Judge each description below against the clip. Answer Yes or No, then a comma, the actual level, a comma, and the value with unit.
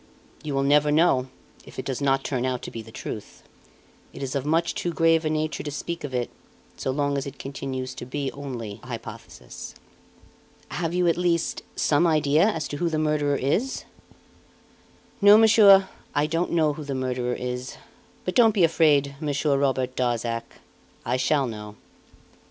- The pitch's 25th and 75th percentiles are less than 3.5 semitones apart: No, average, 4.0 semitones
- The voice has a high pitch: No, medium, 145 Hz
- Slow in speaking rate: No, average, 180 wpm